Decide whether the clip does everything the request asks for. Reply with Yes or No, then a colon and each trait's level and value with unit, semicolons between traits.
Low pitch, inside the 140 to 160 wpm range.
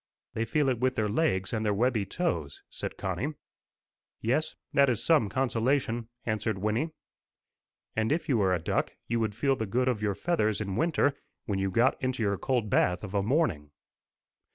No: low, 115 Hz; average, 185 wpm